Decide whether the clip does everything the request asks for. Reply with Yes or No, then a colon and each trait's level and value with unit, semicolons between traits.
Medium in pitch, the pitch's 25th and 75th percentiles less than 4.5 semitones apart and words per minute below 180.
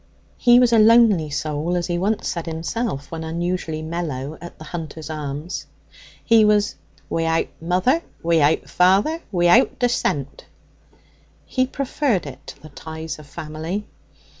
No: medium, 170 Hz; average, 5.2 semitones; average, 140 wpm